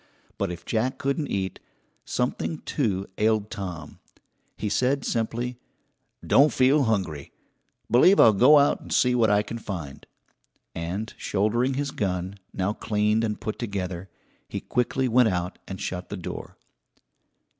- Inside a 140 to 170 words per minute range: Yes, average, 145 wpm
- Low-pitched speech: Yes, low, 110 Hz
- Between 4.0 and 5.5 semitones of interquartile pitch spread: Yes, average, 4.6 semitones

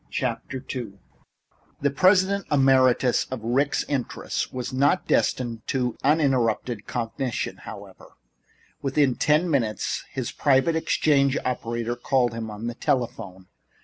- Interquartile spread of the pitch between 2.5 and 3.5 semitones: Yes, average, 3.1 semitones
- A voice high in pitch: No, low, 130 Hz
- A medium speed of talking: No, slow, 115 wpm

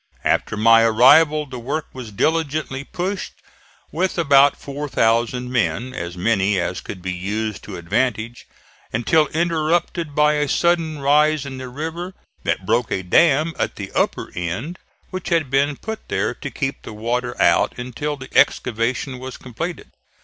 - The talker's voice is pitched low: Yes, low, 130 Hz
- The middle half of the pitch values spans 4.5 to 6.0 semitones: Yes, average, 5.3 semitones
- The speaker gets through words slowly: No, average, 155 wpm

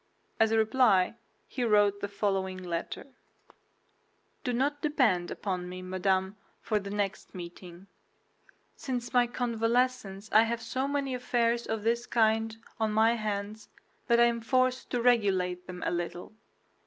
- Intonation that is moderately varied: Yes, average, 3.9 semitones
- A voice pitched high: Yes, high, 220 Hz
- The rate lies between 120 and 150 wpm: Yes, average, 145 wpm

